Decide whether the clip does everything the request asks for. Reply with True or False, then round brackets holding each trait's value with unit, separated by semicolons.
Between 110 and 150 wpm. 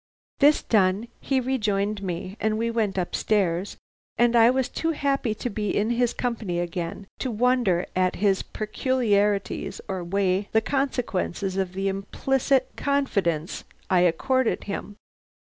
True (140 wpm)